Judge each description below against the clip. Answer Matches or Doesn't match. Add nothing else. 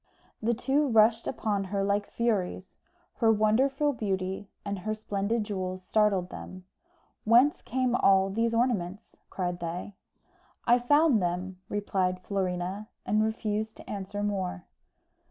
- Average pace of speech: Doesn't match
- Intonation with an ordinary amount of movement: Matches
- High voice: Matches